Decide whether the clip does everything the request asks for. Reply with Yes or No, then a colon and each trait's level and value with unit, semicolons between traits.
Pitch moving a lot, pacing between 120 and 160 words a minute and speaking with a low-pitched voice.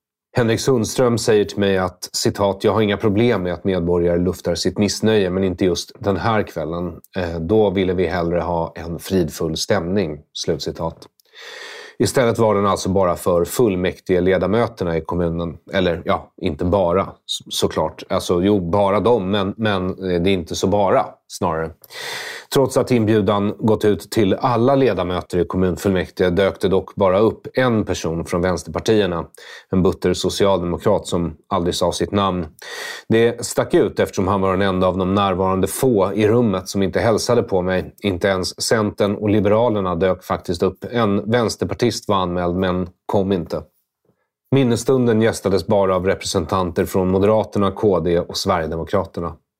No: average, 3.0 semitones; average, 155 wpm; very low, 95 Hz